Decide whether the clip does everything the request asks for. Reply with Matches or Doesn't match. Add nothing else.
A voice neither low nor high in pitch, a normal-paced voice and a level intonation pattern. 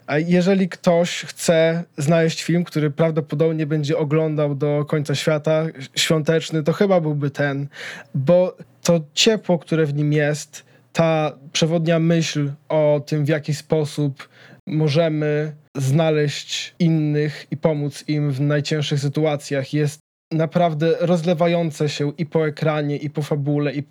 Matches